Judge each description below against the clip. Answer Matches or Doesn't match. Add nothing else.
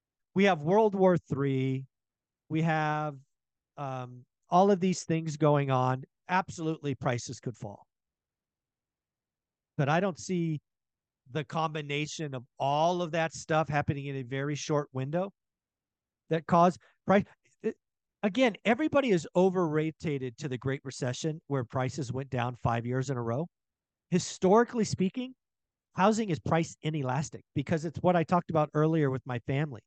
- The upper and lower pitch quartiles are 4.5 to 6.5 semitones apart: Matches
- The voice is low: Doesn't match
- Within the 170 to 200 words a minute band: Doesn't match